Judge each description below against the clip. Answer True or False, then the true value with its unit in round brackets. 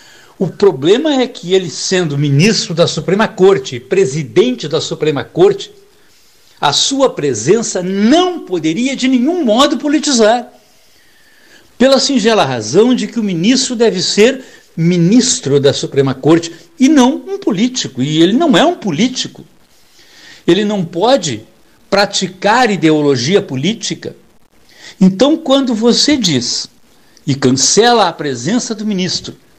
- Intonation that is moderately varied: False (7.5 semitones)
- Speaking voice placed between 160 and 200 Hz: False (210 Hz)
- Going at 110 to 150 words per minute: True (125 wpm)